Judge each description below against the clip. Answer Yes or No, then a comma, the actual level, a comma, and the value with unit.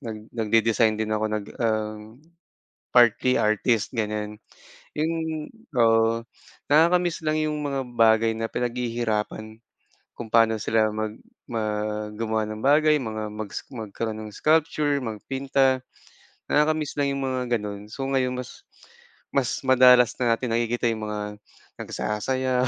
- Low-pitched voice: Yes, low, 115 Hz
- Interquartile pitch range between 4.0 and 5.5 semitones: No, average, 3.6 semitones